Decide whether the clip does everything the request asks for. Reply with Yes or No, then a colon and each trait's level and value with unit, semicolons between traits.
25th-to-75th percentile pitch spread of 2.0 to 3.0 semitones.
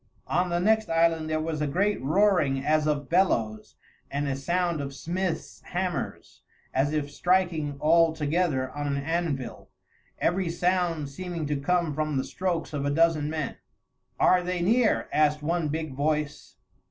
No: average, 3.4 semitones